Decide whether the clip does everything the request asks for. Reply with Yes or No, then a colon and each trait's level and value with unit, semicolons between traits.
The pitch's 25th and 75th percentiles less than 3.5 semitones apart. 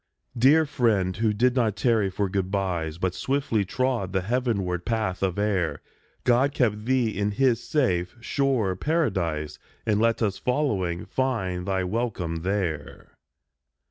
No: average, 4.9 semitones